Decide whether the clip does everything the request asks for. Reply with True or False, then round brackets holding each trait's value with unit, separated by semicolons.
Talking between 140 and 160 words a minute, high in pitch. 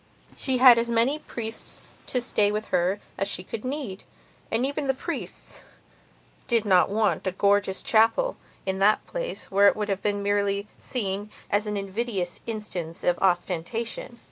True (150 wpm; 210 Hz)